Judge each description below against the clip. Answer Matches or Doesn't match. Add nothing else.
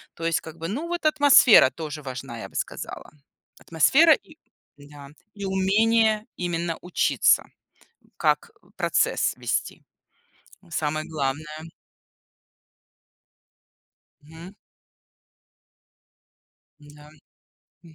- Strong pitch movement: Matches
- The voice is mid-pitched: Matches